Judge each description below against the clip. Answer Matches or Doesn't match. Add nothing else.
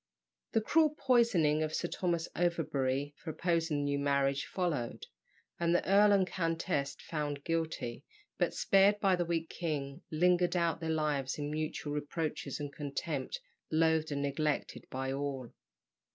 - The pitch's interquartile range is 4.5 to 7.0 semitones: Doesn't match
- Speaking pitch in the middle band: Matches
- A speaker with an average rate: Matches